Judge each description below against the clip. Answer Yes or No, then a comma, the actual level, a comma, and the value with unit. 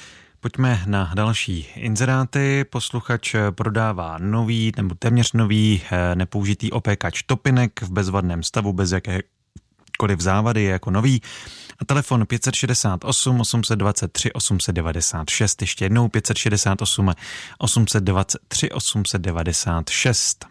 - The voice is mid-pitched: No, low, 105 Hz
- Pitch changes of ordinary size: Yes, average, 3.8 semitones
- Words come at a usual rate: No, slow, 95 wpm